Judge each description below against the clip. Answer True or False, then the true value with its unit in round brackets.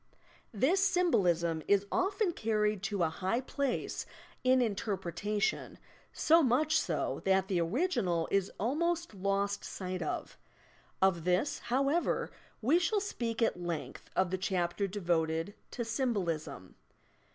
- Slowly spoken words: True (130 wpm)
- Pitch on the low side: False (205 Hz)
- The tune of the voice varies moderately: False (6.9 semitones)